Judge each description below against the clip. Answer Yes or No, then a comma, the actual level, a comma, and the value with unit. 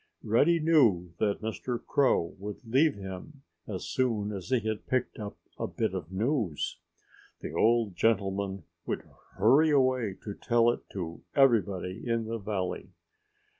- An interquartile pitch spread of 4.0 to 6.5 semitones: Yes, average, 4.8 semitones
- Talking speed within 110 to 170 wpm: Yes, average, 145 wpm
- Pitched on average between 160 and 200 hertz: No, low, 110 Hz